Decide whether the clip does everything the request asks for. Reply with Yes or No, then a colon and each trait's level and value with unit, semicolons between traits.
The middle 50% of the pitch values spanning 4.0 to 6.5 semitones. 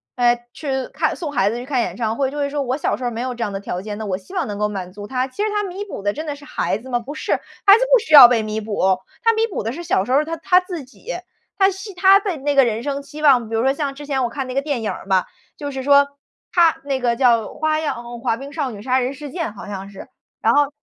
Yes: average, 4.8 semitones